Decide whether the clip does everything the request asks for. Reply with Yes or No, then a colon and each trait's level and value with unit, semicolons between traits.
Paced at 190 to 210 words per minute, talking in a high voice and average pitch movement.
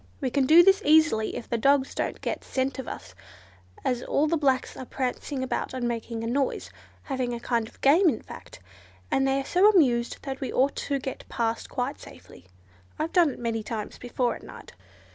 Yes: fast, 205 wpm; very high, 260 Hz; average, 3.1 semitones